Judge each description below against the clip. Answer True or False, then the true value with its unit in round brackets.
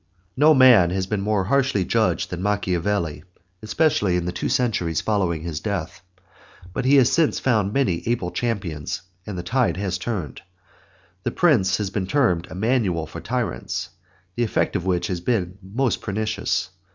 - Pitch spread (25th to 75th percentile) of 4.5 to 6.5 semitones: True (5.1 semitones)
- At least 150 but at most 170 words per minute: True (165 wpm)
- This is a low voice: True (100 Hz)